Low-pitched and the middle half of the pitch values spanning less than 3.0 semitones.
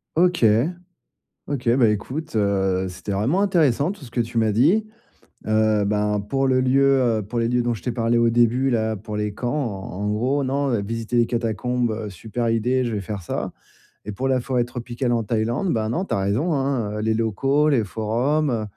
No: low, 120 Hz; average, 3.8 semitones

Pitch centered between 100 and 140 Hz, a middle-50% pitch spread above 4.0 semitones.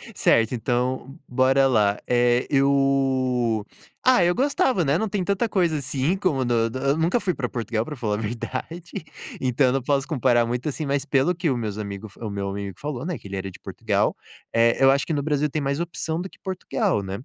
Yes: low, 135 Hz; average, 4.7 semitones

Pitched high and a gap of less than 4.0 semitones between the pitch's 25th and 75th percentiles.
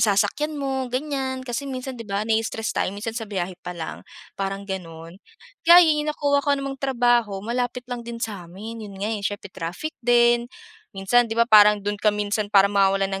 No: high, 225 Hz; average, 4.3 semitones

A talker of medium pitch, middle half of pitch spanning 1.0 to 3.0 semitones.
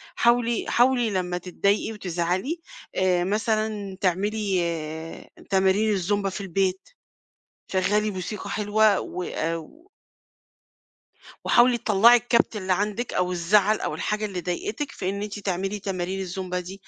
No: high, 200 Hz; average, 2.7 semitones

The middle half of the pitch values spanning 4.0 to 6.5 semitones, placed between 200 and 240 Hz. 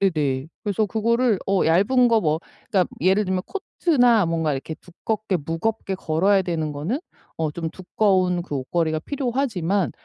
No: average, 5.1 semitones; medium, 185 Hz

